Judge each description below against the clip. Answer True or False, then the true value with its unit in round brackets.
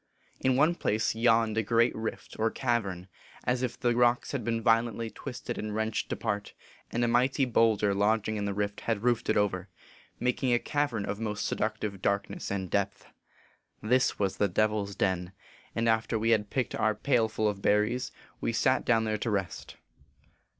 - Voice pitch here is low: True (110 Hz)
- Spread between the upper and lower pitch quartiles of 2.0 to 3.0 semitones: True (2.6 semitones)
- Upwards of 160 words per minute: True (185 wpm)